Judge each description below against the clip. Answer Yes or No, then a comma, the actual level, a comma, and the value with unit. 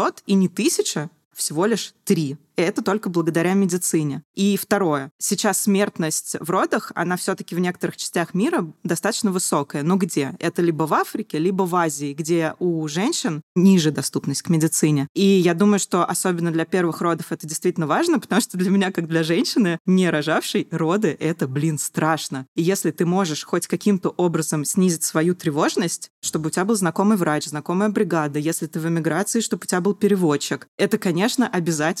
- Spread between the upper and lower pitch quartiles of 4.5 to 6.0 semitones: No, average, 3.6 semitones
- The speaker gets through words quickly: Yes, fast, 180 wpm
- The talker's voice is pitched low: No, medium, 175 Hz